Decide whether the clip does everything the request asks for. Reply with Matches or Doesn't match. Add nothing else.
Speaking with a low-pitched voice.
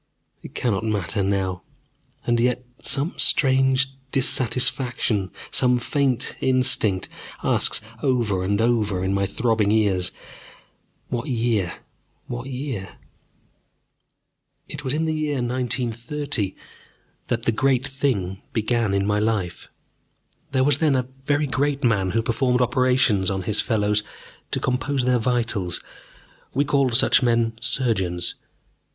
Matches